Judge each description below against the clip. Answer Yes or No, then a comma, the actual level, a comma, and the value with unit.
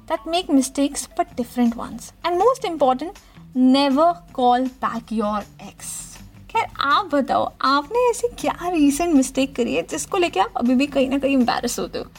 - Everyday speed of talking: Yes, average, 175 wpm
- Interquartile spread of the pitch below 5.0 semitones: No, wide, 5.5 semitones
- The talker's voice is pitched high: Yes, very high, 275 Hz